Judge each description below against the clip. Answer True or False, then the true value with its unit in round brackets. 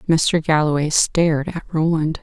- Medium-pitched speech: True (155 Hz)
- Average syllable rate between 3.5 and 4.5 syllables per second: True (4.4 syllables/s)